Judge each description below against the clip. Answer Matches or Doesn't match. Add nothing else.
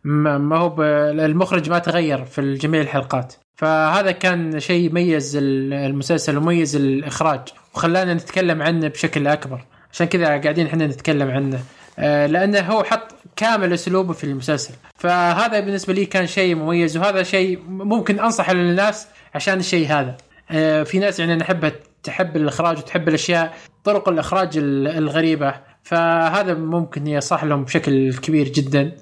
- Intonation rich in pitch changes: Doesn't match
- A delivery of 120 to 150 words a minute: Matches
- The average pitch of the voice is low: Doesn't match